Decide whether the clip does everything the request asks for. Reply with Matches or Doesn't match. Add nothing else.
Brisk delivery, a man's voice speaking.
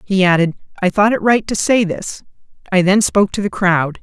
Doesn't match